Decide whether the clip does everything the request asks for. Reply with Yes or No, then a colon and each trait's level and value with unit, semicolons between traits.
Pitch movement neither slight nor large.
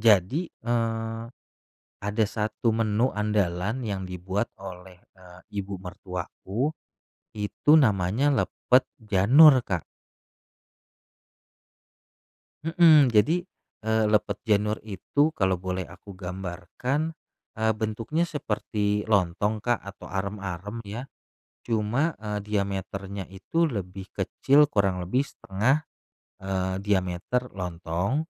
Yes: average, 3.9 semitones